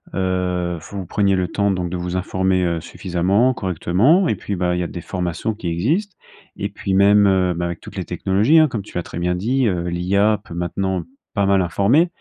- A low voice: Yes, very low, 95 Hz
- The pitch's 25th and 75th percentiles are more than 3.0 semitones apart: No, narrow, 2.6 semitones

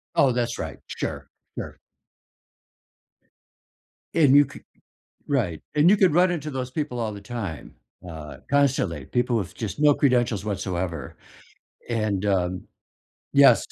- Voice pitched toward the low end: Yes, low, 120 Hz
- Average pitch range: No, wide, 7.1 semitones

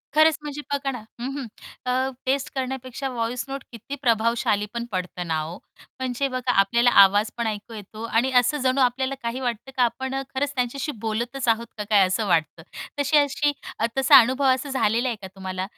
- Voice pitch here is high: Yes, high, 245 Hz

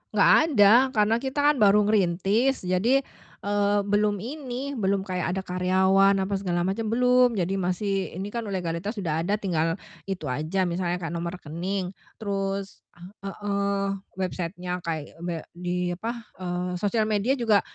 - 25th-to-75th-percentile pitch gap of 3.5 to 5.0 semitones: No, average, 2.7 semitones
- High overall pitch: Yes, high, 195 Hz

